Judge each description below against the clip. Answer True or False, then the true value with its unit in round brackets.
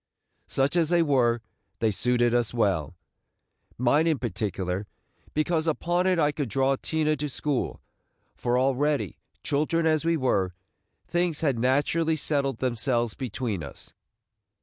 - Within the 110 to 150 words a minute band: True (140 wpm)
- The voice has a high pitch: False (135 Hz)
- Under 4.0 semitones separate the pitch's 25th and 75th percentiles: False (4.8 semitones)